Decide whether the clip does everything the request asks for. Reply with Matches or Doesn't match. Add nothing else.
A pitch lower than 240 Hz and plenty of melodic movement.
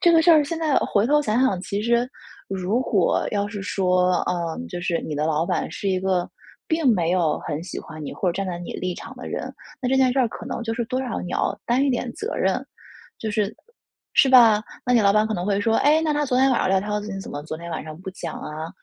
Matches